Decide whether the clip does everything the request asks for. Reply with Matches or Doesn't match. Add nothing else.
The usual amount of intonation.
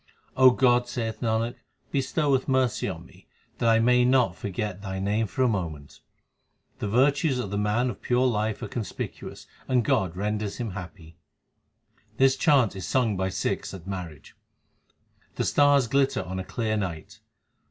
Matches